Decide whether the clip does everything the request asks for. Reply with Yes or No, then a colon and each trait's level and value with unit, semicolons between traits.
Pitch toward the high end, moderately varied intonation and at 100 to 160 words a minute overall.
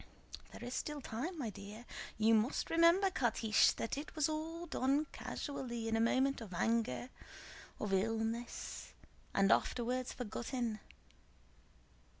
Yes: high, 240 Hz; average, 4.4 semitones; slow, 135 wpm